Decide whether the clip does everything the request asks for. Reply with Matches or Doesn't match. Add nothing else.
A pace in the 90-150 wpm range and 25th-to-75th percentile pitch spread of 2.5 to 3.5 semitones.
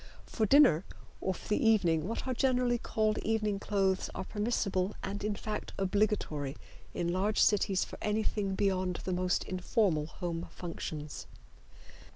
Matches